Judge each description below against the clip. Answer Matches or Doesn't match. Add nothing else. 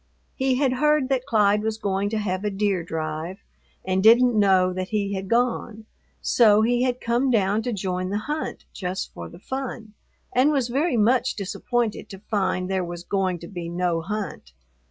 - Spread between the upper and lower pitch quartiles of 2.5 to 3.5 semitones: Doesn't match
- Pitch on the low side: Doesn't match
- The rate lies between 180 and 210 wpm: Matches